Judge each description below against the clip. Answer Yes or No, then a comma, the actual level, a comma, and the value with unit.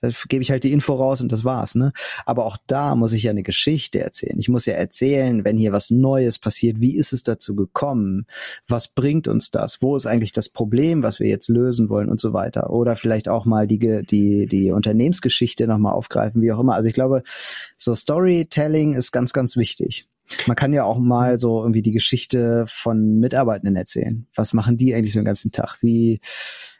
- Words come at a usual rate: No, fast, 215 wpm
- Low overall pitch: Yes, low, 115 Hz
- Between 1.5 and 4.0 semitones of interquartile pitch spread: Yes, average, 2.9 semitones